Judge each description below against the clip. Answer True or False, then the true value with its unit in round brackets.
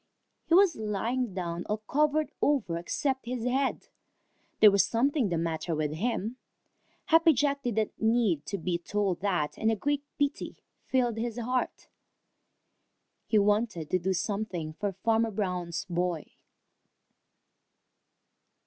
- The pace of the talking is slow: True (130 wpm)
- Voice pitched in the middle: False (215 Hz)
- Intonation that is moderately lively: False (5.8 semitones)